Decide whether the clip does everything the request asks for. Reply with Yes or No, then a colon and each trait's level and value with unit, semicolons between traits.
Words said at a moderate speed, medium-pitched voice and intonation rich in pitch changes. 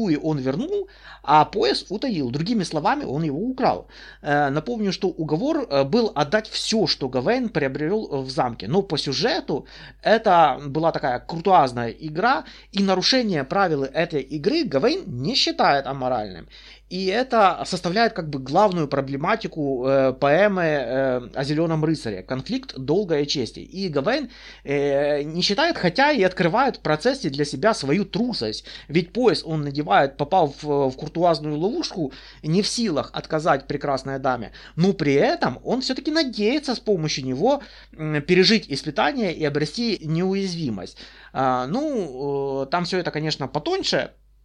Yes: average, 145 wpm; medium, 155 Hz; wide, 6.7 semitones